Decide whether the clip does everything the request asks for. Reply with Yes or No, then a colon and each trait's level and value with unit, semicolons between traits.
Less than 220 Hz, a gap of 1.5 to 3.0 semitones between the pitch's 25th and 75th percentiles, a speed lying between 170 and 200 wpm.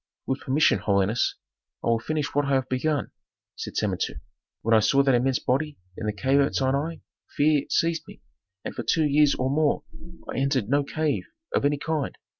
Yes: medium, 140 Hz; average, 2.7 semitones; average, 190 wpm